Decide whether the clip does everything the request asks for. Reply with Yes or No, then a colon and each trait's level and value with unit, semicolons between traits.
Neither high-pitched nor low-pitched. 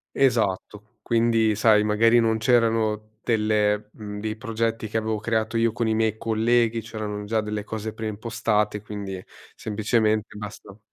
No: low, 110 Hz